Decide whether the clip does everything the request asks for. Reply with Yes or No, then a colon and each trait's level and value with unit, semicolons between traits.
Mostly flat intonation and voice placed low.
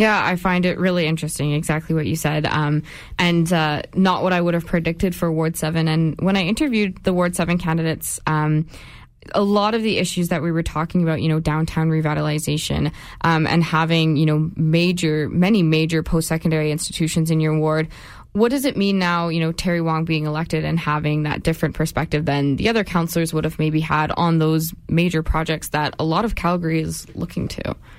No: narrow, 2.0 semitones; medium, 160 Hz